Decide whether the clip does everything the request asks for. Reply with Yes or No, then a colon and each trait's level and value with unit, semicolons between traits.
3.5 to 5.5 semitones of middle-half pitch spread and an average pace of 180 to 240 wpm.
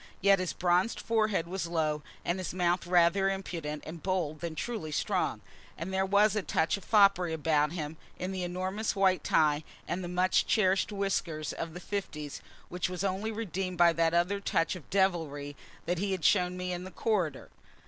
No: average, 2.7 semitones; average, 190 wpm